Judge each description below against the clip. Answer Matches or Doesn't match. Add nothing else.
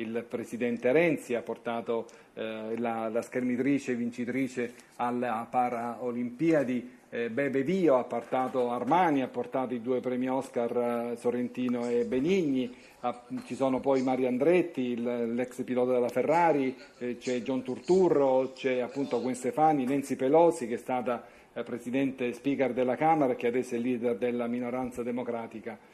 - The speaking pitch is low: Matches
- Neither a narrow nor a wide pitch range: Doesn't match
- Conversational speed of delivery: Matches